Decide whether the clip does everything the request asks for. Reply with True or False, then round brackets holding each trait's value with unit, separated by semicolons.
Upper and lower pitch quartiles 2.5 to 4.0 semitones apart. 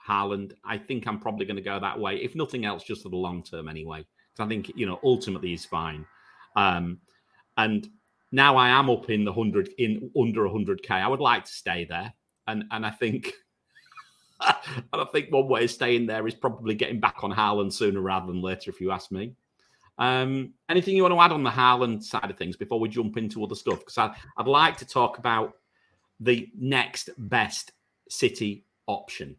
False (4.5 semitones)